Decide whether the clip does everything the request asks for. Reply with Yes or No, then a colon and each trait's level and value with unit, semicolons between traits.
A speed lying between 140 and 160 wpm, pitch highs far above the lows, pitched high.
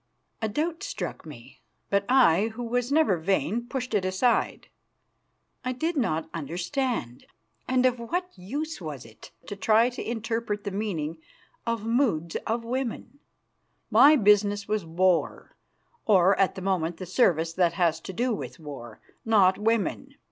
Yes: average, 155 wpm; wide, 5.7 semitones; high, 210 Hz